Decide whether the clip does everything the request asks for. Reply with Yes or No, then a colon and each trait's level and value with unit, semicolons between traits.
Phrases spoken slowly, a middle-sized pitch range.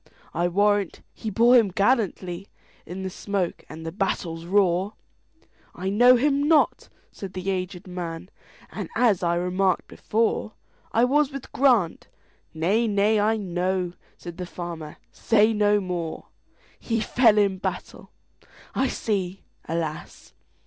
Yes: slow, 115 wpm; average, 3.8 semitones